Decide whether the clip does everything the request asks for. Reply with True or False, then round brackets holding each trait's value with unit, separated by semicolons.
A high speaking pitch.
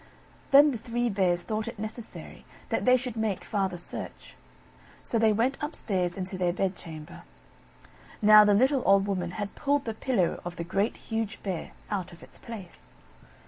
True (205 Hz)